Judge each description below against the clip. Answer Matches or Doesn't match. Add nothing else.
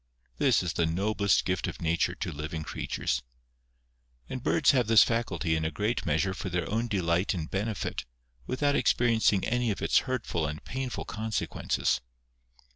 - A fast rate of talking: Doesn't match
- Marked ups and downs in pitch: Matches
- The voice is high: Doesn't match